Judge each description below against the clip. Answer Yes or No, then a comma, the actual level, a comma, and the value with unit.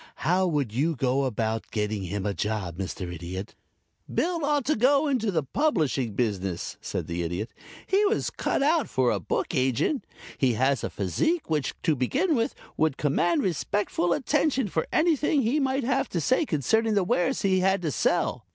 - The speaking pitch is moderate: Yes, medium, 160 Hz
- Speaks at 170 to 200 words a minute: Yes, average, 180 wpm